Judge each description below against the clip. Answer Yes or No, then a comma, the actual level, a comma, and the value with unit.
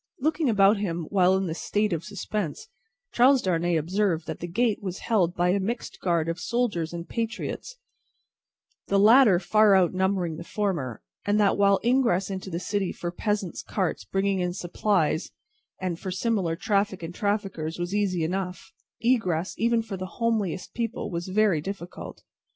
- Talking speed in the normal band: Yes, average, 165 wpm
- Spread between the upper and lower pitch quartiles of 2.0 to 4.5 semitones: Yes, average, 3.4 semitones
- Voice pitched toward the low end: No, high, 190 Hz